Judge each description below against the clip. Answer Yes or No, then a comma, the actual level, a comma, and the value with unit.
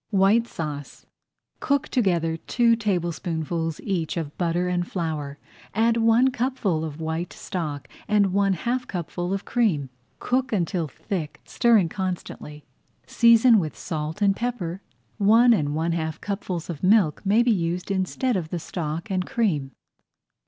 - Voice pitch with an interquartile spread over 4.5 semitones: Yes, wide, 5.4 semitones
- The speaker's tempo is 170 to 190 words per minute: No, average, 145 wpm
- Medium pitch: Yes, medium, 180 Hz